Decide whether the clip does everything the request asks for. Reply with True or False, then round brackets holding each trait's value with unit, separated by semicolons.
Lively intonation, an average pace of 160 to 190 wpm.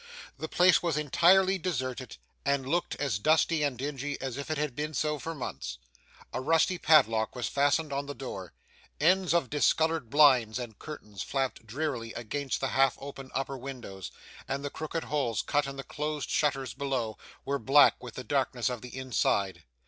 False (3.2 semitones; 180 wpm)